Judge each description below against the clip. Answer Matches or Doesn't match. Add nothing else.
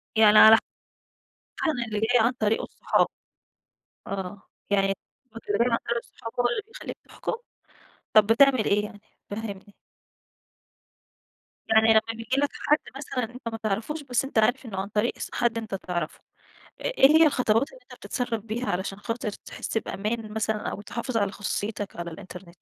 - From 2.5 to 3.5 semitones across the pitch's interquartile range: Matches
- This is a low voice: Doesn't match